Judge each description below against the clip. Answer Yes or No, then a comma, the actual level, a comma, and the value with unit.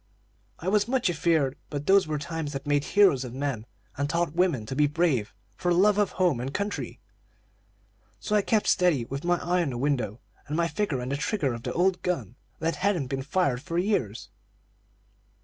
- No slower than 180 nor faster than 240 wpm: Yes, average, 200 wpm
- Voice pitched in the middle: Yes, medium, 155 Hz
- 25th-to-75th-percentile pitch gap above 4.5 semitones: Yes, average, 5.2 semitones